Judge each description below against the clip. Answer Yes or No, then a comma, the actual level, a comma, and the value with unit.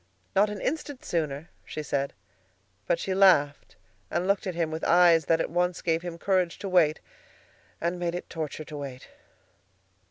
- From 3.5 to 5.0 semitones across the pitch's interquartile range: No, average, 2.9 semitones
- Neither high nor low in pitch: Yes, medium, 170 Hz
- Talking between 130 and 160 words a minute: No, average, 170 wpm